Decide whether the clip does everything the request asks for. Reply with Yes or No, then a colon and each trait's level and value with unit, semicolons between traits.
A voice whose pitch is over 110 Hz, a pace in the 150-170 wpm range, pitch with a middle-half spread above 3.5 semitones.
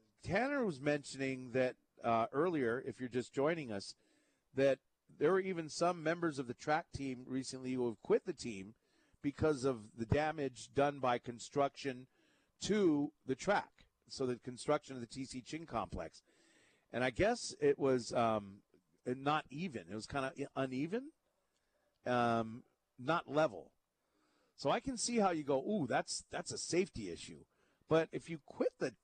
Yes: low, 135 Hz; average, 165 wpm; average, 4.0 semitones